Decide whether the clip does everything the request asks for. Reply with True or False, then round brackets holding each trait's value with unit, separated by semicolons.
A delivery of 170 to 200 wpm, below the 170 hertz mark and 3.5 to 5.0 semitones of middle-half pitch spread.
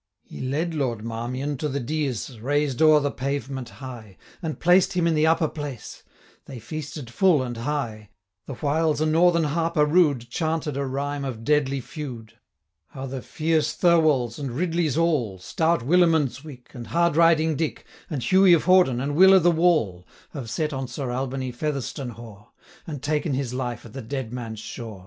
True (175 wpm; 140 Hz; 4.4 semitones)